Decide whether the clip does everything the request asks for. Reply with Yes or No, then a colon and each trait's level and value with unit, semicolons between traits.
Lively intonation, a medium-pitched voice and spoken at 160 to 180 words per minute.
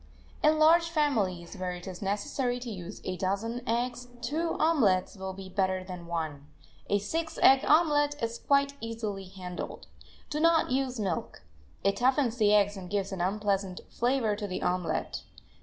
No: wide, 6.1 semitones; high, 210 Hz; average, 165 wpm